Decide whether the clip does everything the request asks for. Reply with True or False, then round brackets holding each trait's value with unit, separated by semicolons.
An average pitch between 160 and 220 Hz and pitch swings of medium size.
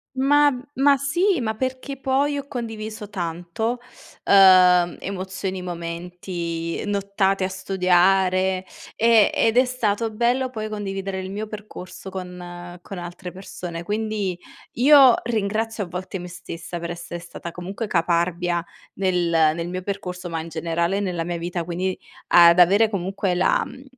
True (190 Hz; 3.7 semitones)